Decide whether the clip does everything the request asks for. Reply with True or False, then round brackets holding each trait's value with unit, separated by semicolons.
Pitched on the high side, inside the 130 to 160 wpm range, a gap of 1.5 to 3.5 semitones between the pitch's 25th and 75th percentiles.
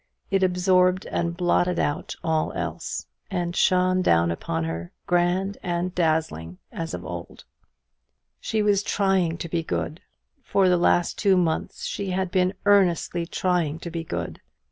False (175 Hz; 150 wpm; 2.4 semitones)